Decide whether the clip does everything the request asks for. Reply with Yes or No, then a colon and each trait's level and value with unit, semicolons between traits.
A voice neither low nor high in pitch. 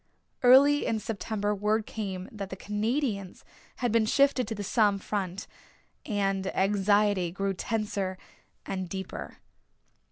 No: high, 205 Hz